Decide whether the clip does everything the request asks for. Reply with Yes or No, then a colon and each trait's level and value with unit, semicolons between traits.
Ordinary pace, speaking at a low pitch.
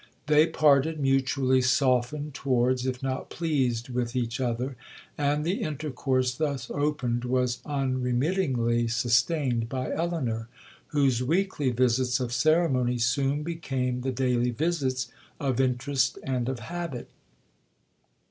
No: slow, 120 wpm; low, 130 Hz